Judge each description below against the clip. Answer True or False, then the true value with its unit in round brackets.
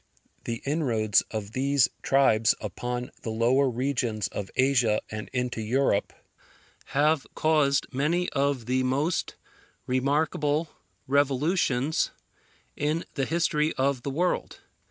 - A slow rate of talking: True (115 wpm)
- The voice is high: False (135 Hz)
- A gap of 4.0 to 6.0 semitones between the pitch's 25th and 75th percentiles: False (3.3 semitones)